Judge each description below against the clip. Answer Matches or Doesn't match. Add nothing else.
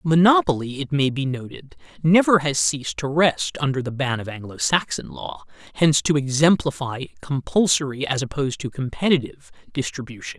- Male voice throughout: Matches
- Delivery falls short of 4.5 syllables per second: Doesn't match